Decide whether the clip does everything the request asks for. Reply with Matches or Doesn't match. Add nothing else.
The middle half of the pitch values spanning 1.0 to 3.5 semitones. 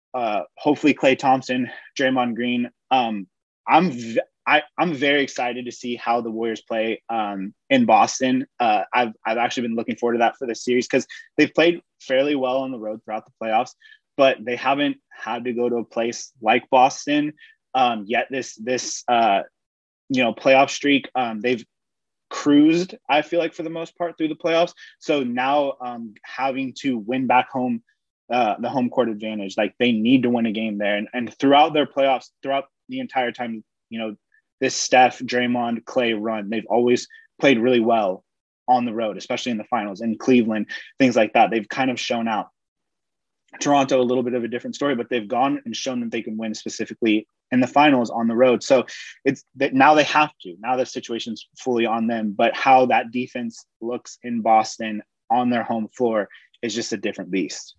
Matches